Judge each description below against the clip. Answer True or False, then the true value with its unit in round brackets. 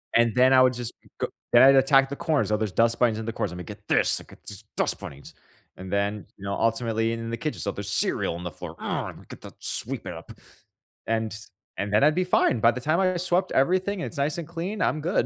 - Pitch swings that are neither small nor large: False (6.2 semitones)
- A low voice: True (120 Hz)